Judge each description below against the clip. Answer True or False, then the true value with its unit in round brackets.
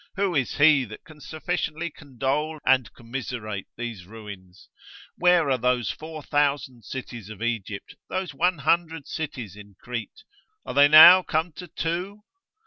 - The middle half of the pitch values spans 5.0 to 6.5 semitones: True (5.6 semitones)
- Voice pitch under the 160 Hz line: True (140 Hz)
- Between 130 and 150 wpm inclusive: True (135 wpm)